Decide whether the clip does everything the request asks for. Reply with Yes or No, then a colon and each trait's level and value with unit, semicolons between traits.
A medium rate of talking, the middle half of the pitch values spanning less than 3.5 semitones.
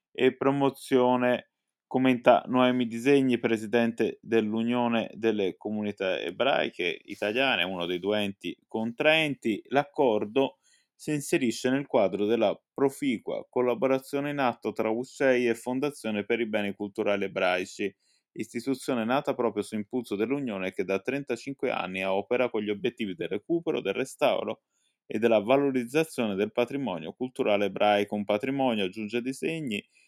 No: average, 130 wpm; average, 4.1 semitones